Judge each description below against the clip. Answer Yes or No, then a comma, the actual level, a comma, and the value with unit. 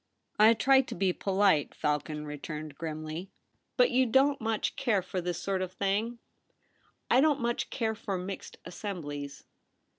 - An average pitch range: No, wide, 6.5 semitones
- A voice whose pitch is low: No, high, 195 Hz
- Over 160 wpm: Yes, average, 175 wpm